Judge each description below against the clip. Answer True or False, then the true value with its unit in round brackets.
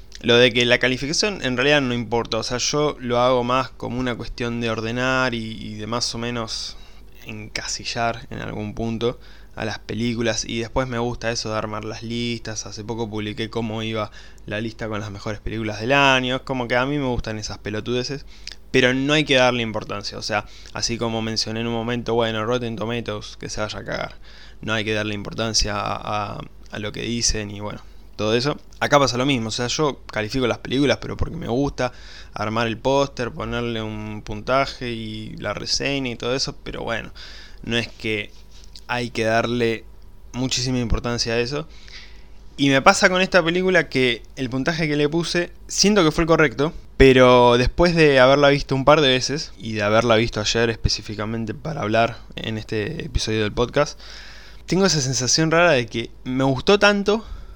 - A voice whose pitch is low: True (115 Hz)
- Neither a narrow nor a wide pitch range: True (3.3 semitones)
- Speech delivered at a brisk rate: True (195 wpm)